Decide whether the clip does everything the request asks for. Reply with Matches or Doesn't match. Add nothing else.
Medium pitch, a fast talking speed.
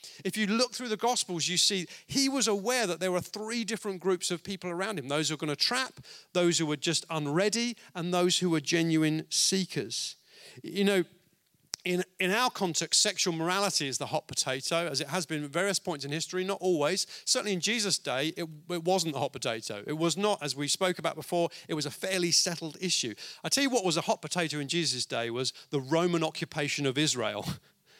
Matches